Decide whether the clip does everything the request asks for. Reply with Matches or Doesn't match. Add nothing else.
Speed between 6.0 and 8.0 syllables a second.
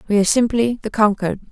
Matches